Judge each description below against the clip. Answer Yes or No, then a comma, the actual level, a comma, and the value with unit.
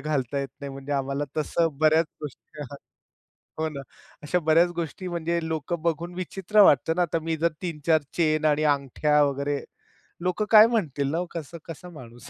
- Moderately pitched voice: Yes, medium, 155 Hz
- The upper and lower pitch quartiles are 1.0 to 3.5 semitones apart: Yes, average, 3.1 semitones